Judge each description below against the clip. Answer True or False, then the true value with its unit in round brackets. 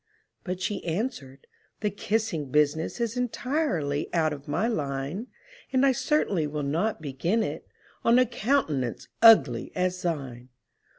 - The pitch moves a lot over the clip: True (8.0 semitones)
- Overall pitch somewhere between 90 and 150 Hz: False (175 Hz)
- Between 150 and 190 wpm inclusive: False (135 wpm)